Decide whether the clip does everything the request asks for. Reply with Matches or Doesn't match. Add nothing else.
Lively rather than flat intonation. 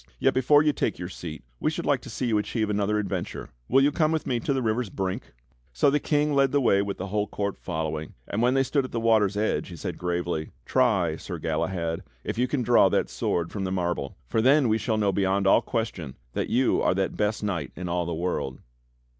Matches